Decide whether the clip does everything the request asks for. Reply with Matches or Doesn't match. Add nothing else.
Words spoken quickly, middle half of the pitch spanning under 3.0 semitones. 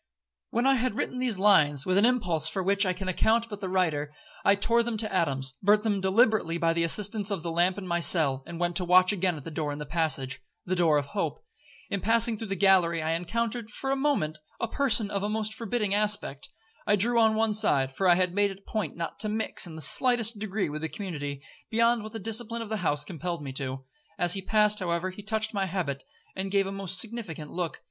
Doesn't match